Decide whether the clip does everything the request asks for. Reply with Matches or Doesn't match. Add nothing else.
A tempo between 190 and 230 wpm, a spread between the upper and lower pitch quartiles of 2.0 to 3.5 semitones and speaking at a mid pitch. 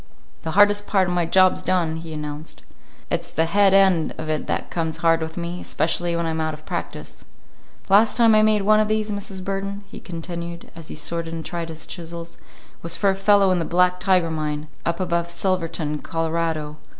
Matches